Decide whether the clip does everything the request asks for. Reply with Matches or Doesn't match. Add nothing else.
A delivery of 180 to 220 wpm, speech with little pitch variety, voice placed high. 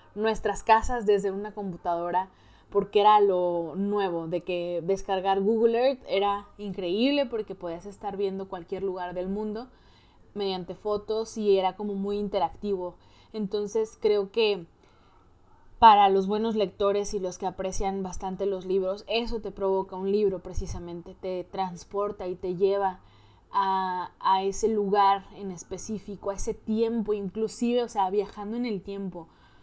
Doesn't match